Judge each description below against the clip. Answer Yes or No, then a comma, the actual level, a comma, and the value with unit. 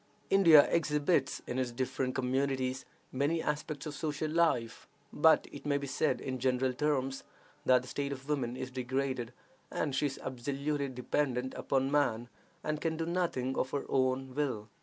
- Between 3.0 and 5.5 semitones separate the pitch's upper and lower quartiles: No, narrow, 2.5 semitones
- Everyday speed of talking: Yes, average, 165 wpm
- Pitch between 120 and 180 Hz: Yes, low, 135 Hz